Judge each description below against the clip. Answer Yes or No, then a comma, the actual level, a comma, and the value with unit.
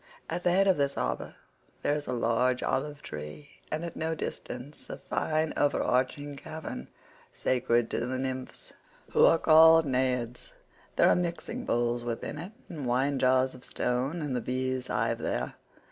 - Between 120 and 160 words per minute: No, average, 170 wpm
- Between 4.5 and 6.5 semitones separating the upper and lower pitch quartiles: No, average, 3.9 semitones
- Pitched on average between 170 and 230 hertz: No, low, 130 Hz